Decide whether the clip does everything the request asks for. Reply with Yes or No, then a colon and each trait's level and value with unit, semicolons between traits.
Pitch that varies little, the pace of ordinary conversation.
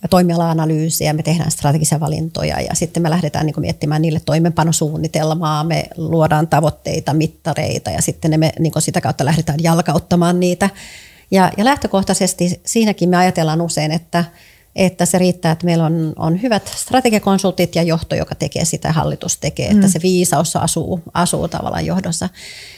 Yes: narrow, 2.1 semitones; average, 135 wpm